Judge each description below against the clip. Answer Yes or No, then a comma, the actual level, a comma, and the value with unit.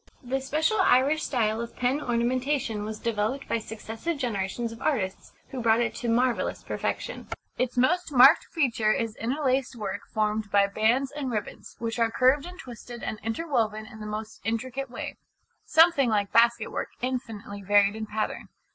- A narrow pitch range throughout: No, average, 3.4 semitones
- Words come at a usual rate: Yes, average, 165 wpm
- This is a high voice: Yes, high, 235 Hz